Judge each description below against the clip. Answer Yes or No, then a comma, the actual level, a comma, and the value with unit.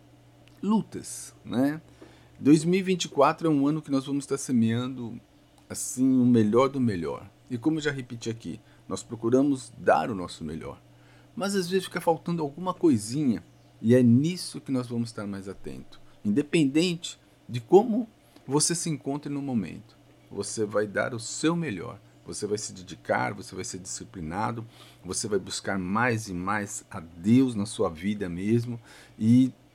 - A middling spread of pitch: No, wide, 6.4 semitones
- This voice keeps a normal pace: Yes, average, 160 wpm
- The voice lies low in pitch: Yes, low, 120 Hz